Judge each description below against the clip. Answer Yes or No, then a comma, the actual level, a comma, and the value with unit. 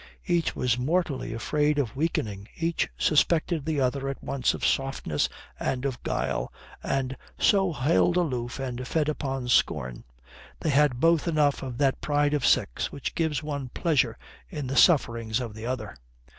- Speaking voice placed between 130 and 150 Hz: Yes, medium, 140 Hz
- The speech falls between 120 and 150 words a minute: No, average, 160 wpm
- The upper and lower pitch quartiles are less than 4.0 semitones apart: Yes, average, 3.6 semitones